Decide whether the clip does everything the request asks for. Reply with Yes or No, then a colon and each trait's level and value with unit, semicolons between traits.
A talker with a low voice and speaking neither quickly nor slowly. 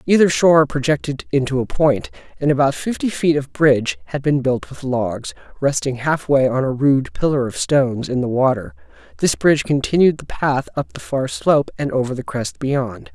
Yes: low, 125 Hz; average, 190 wpm